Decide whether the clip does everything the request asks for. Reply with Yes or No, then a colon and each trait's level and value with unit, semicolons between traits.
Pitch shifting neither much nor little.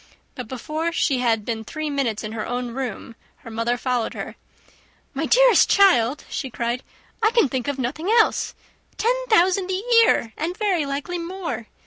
No: wide, 7.4 semitones